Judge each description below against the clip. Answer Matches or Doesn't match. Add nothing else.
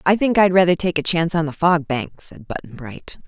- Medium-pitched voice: Matches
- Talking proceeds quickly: Matches